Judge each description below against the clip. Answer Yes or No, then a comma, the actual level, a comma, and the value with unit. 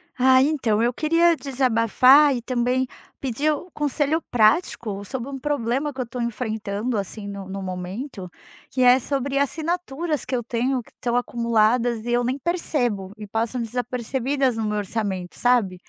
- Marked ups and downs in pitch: No, average, 3.7 semitones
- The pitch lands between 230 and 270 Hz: Yes, high, 245 Hz